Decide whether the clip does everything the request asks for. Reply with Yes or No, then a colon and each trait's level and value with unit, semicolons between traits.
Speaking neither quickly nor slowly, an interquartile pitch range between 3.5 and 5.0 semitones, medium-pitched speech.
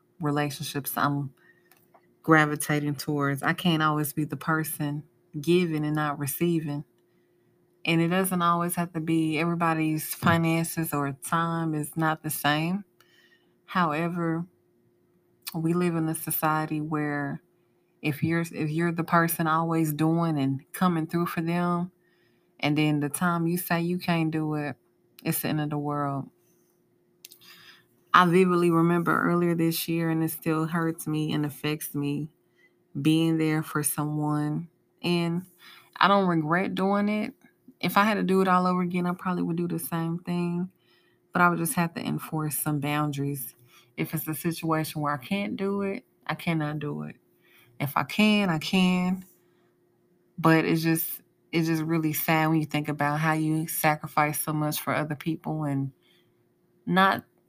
No: average, 160 wpm; narrow, 2.5 semitones; medium, 160 Hz